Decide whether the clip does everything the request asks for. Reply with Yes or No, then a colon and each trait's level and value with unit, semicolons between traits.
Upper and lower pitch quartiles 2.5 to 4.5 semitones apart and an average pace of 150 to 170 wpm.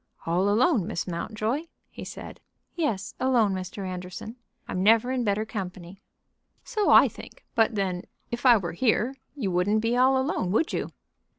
No: average, 5.0 semitones; average, 165 wpm